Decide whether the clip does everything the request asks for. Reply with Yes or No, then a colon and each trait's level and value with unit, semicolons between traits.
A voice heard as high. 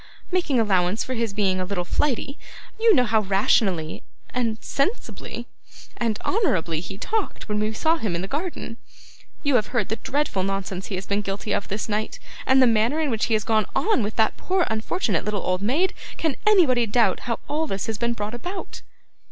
Yes: high, 220 Hz